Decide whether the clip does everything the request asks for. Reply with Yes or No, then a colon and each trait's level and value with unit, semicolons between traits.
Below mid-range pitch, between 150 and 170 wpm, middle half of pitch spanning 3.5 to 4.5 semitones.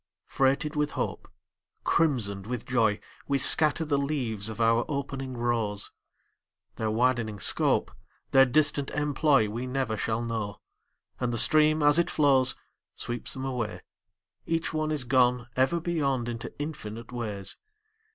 No: low, 130 Hz; average, 140 wpm; average, 4.2 semitones